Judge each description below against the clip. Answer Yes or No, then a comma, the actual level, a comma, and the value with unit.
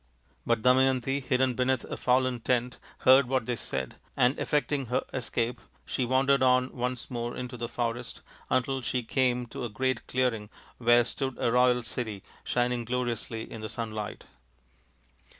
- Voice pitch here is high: No, low, 125 Hz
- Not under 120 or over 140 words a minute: No, average, 155 wpm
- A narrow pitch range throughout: Yes, narrow, 1.6 semitones